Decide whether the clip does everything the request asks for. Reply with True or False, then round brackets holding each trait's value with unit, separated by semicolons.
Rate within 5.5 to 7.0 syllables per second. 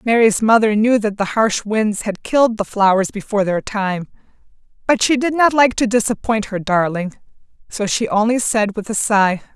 False (4.9 syllables/s)